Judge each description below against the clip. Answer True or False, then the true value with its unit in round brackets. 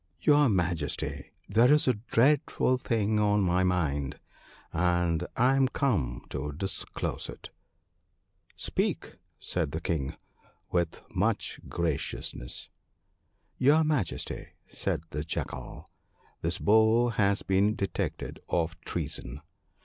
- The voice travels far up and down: True (6.1 semitones)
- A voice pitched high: False (95 Hz)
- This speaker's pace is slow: True (120 wpm)